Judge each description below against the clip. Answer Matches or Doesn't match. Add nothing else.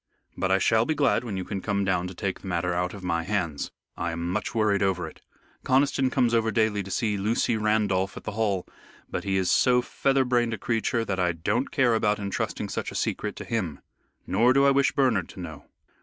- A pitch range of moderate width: Matches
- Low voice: Matches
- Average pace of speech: Doesn't match